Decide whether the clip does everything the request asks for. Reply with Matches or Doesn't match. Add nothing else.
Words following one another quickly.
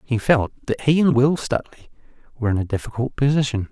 Doesn't match